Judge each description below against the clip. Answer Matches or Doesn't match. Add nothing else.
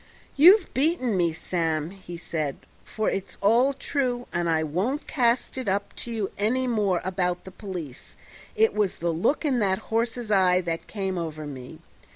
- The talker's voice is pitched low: Doesn't match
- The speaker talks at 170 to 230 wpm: Matches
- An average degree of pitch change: Doesn't match